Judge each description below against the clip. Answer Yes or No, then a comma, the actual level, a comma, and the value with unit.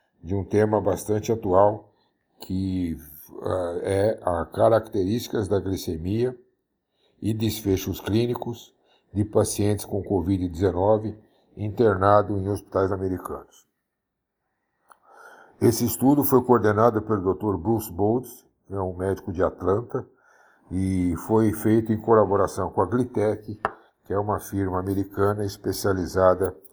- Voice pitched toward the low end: Yes, low, 105 Hz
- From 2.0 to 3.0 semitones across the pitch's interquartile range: Yes, narrow, 2.5 semitones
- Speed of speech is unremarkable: No, slow, 110 wpm